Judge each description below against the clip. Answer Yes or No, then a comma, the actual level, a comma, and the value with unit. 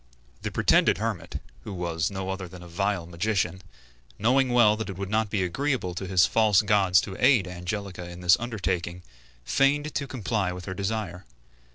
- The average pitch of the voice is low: Yes, very low, 95 Hz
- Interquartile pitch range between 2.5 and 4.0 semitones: Yes, average, 3.5 semitones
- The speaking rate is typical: Yes, average, 180 wpm